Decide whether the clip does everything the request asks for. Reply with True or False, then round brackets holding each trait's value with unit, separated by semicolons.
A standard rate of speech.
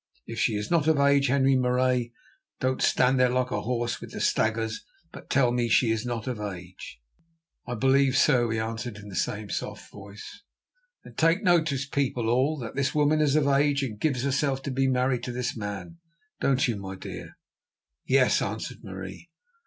True (185 wpm)